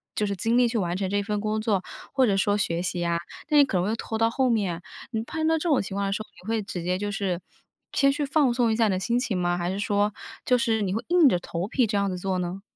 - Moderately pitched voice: No, high, 205 Hz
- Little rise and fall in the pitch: No, average, 4.1 semitones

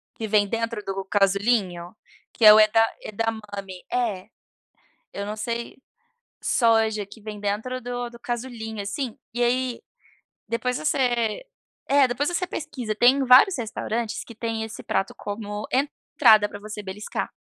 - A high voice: Yes, high, 225 Hz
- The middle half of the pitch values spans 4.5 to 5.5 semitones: No, average, 2.8 semitones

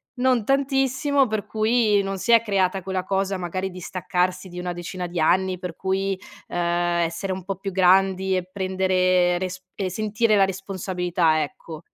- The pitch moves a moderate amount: No, narrow, 1.8 semitones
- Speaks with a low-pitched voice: No, high, 190 Hz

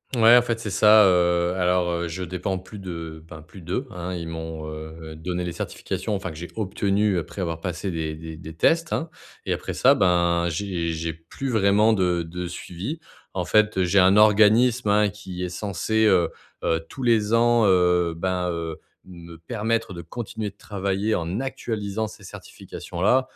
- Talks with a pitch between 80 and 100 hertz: Yes, very low, 95 Hz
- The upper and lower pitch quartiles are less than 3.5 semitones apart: No, average, 3.9 semitones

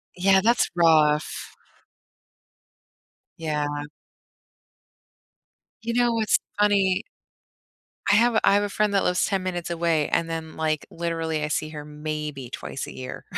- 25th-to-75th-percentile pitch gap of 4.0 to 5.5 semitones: Yes, average, 4.5 semitones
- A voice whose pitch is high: No, medium, 165 Hz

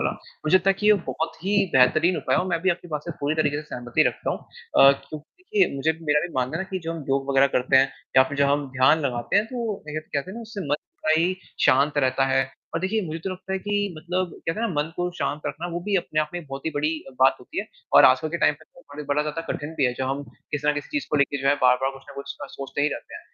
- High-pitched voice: No, medium, 150 Hz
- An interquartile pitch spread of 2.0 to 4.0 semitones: No, average, 4.4 semitones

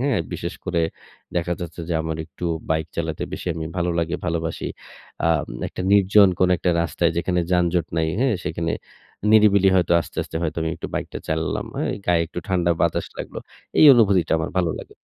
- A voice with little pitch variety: Yes, narrow, 2.2 semitones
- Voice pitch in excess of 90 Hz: No, very low, 85 Hz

